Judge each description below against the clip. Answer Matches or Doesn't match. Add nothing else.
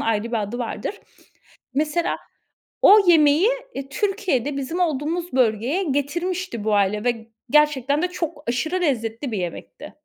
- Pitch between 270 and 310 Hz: Matches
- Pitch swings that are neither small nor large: Doesn't match